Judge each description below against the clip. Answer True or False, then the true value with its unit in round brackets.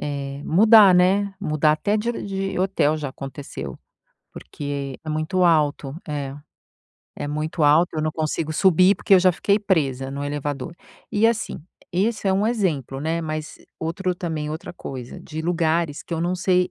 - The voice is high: False (160 Hz)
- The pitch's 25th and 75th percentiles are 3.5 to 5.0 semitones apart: True (4.2 semitones)